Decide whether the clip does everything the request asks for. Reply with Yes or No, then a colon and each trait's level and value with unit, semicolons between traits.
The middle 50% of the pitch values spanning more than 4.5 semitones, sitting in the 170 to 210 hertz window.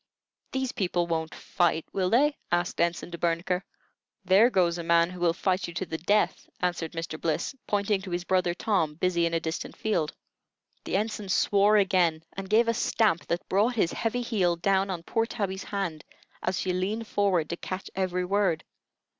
No: average, 3.1 semitones; medium, 185 Hz